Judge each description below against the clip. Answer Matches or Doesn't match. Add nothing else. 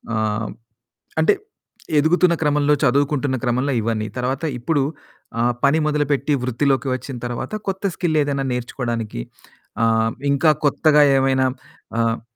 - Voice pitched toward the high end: Doesn't match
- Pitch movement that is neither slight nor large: Matches